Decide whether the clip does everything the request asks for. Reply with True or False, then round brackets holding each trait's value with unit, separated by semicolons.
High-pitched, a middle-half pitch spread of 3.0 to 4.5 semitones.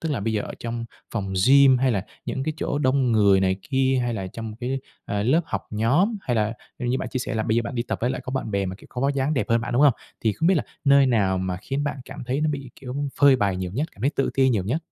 False (125 Hz; 4.2 semitones)